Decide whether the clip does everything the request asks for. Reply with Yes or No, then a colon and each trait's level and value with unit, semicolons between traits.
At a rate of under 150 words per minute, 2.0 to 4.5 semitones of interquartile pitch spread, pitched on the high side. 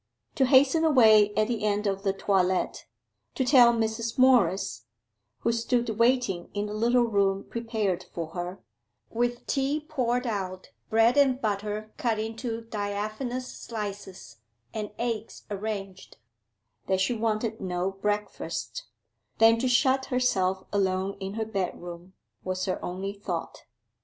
Yes: slow, 135 wpm; average, 3.7 semitones; high, 215 Hz